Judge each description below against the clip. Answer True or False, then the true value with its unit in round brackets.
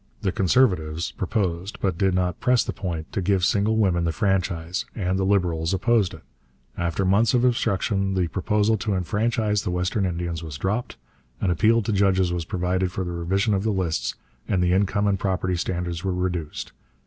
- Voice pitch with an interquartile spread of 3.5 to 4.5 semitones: False (2.5 semitones)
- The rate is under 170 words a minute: False (185 wpm)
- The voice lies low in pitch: True (95 Hz)